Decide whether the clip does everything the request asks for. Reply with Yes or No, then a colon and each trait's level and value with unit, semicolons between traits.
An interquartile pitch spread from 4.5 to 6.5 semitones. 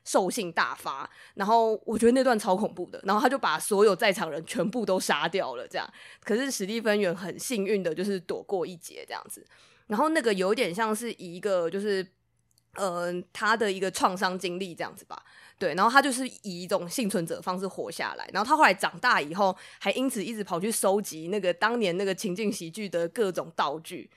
No: average, 3.3 semitones